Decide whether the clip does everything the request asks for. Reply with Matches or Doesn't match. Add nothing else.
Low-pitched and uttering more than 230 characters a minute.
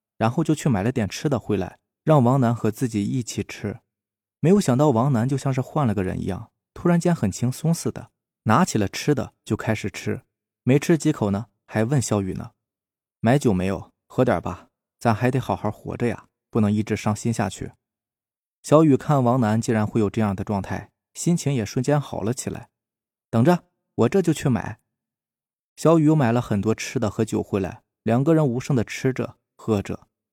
Matches